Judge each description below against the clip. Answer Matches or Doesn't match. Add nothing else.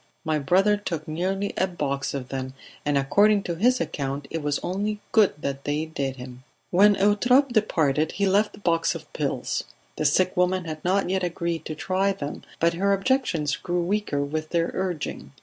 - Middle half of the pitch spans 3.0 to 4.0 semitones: Doesn't match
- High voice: Doesn't match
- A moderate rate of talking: Matches